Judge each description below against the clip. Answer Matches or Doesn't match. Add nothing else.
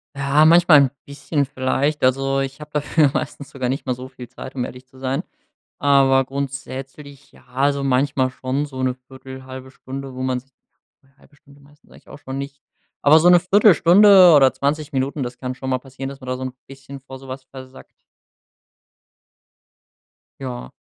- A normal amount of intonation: Doesn't match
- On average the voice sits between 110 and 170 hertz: Matches